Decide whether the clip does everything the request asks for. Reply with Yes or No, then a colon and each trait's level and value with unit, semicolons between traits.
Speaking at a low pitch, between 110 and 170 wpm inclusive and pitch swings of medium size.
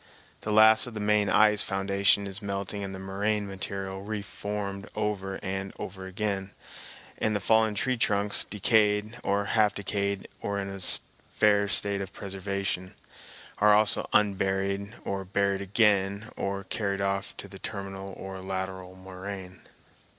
No: low, 100 Hz; average, 150 wpm; narrow, 1.2 semitones